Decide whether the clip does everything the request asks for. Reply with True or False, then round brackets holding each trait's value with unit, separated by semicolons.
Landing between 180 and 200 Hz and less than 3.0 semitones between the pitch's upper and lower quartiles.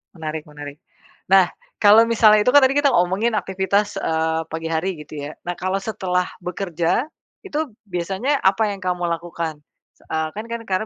False (185 Hz; 4.2 semitones)